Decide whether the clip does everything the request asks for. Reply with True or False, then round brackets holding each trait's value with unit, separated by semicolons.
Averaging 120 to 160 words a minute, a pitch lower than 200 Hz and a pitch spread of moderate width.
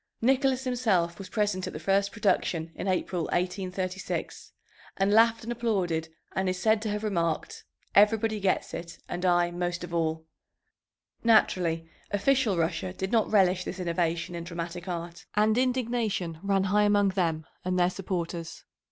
True (155 wpm; 185 Hz; 3.5 semitones)